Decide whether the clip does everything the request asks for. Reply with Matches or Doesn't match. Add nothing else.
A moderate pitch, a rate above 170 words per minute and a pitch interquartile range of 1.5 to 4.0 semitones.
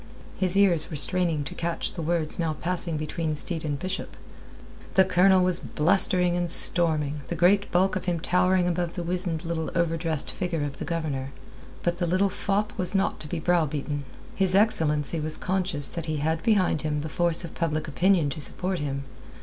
Matches